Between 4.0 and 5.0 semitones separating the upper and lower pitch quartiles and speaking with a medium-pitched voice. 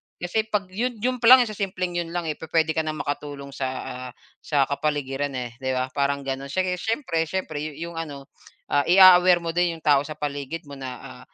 Yes: average, 4.3 semitones; medium, 155 Hz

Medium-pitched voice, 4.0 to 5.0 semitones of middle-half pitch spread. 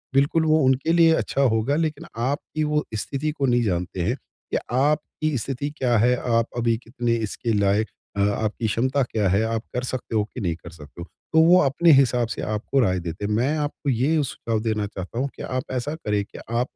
No: low, 120 Hz; average, 4.5 semitones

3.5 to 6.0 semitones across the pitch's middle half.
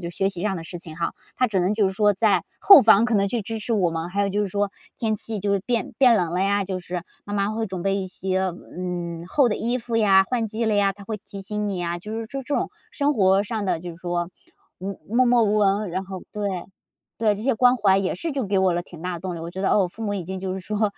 No: average, 3.0 semitones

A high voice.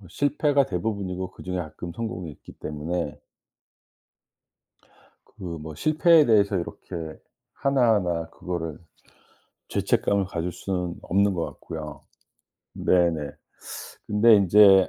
No: very low, 90 Hz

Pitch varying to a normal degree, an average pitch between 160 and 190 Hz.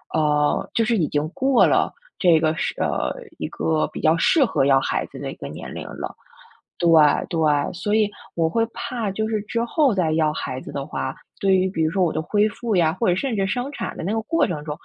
No: wide, 5.9 semitones; medium, 185 Hz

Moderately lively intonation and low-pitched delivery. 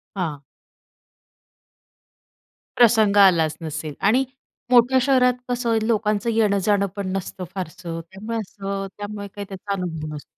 No: average, 3.4 semitones; high, 200 Hz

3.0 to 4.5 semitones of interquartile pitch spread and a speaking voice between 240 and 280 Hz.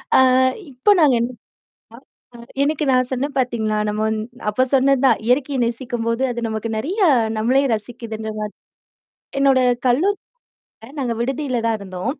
Yes: average, 3.5 semitones; high, 245 Hz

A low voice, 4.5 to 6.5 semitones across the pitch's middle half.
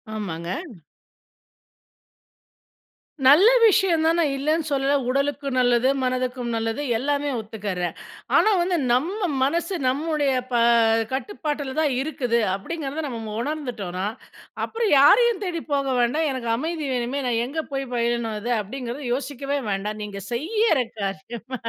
No: very high, 270 Hz; average, 4.8 semitones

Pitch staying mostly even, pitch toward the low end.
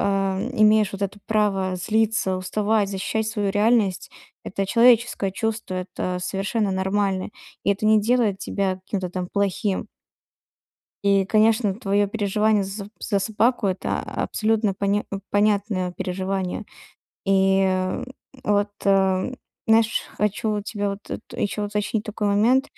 No: narrow, 2.0 semitones; high, 200 Hz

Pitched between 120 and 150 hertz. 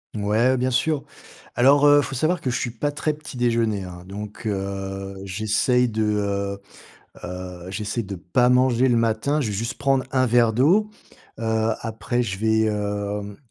No: low, 110 Hz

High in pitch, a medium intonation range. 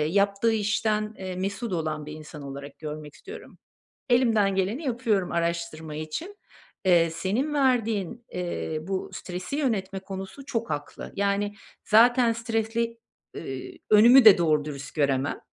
No: high, 195 Hz; wide, 6.1 semitones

